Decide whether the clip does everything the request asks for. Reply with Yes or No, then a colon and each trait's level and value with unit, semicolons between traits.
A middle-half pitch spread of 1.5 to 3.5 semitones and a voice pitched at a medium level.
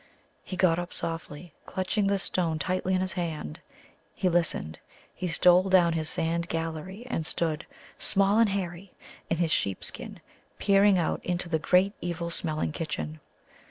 Yes: narrow, 2.4 semitones; medium, 175 Hz